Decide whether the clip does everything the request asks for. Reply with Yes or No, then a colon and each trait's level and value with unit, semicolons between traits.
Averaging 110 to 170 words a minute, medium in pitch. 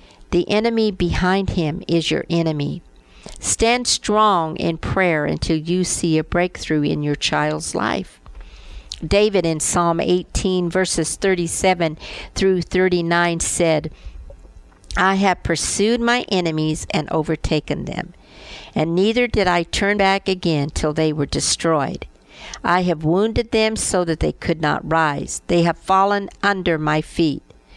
Yes: average, 140 wpm; medium, 175 Hz